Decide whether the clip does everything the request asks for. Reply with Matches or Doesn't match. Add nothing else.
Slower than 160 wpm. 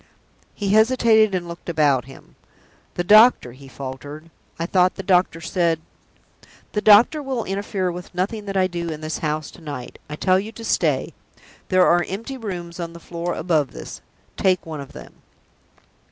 Doesn't match